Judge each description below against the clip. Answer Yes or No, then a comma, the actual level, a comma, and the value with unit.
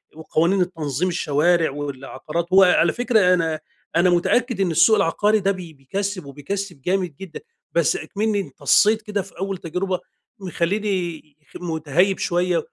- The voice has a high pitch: No, medium, 180 Hz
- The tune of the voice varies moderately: Yes, average, 3.4 semitones